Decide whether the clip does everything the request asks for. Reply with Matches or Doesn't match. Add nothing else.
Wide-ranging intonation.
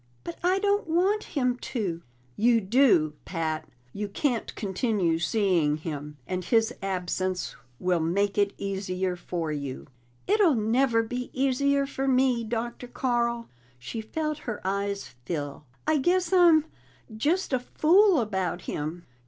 Matches